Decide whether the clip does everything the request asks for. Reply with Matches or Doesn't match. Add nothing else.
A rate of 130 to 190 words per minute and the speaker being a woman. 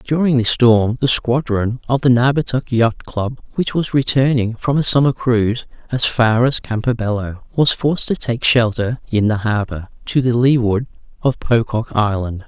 Doesn't match